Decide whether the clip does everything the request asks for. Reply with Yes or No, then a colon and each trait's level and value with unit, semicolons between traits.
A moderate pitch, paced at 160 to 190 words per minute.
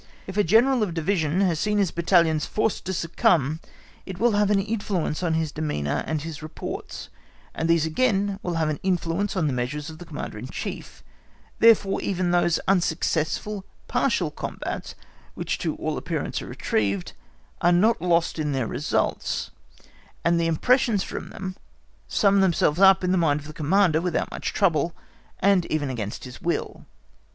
Yes: medium, 170 Hz; average, 170 wpm